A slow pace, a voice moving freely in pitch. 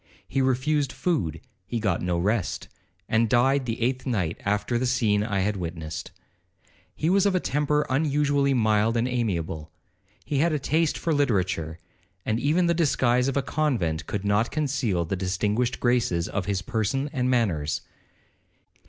No: average, 160 wpm; wide, 6.2 semitones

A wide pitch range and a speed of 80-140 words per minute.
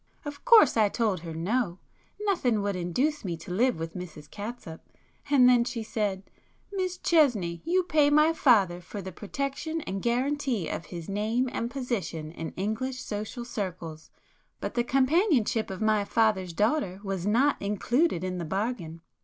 No: wide, 6.3 semitones; average, 155 wpm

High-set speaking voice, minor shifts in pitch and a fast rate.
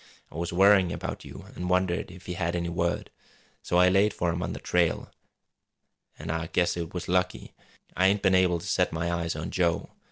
No: very low, 90 Hz; narrow, 1.3 semitones; fast, 215 wpm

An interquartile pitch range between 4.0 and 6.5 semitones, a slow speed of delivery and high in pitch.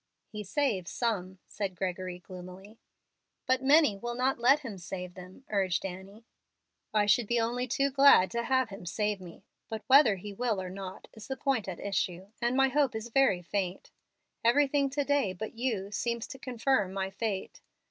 No: average, 5.2 semitones; average, 180 wpm; high, 215 Hz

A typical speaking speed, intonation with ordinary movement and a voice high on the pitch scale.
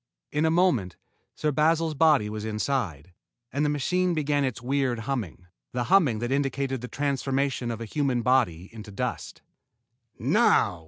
No: average, 155 wpm; average, 4.7 semitones; low, 135 Hz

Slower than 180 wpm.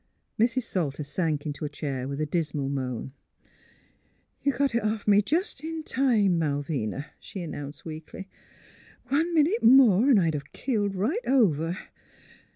Yes: average, 170 wpm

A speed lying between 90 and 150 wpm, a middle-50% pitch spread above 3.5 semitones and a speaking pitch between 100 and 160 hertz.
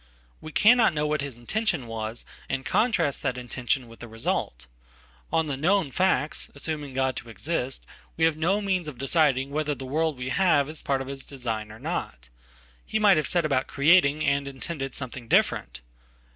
No: average, 170 wpm; average, 4.1 semitones; medium, 140 Hz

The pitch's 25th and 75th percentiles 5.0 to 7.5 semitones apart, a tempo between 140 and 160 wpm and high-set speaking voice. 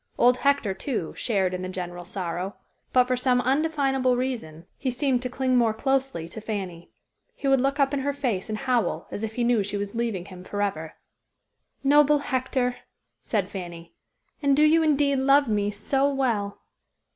No: average, 5.3 semitones; average, 180 wpm; high, 245 Hz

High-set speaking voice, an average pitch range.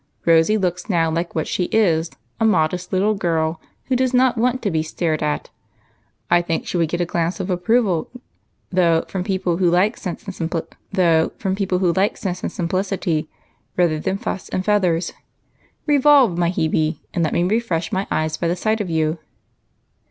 No: medium, 180 Hz; average, 3.1 semitones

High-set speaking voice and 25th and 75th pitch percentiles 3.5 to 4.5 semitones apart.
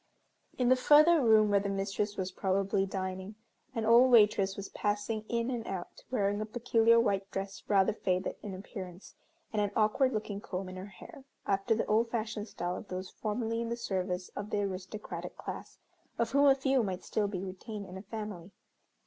No: high, 205 Hz; average, 2.9 semitones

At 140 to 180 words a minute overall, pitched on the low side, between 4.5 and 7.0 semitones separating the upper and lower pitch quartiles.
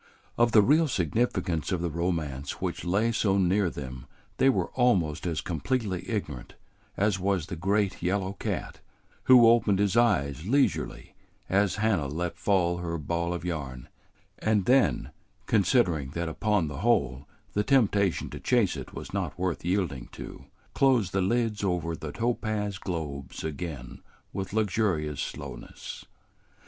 Yes: average, 145 wpm; very low, 95 Hz; average, 4.9 semitones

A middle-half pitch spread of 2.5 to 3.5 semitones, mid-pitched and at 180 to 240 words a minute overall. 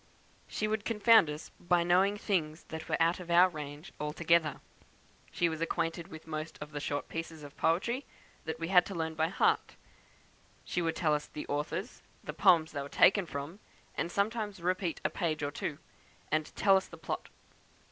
Yes: average, 3.1 semitones; medium, 165 Hz; average, 185 wpm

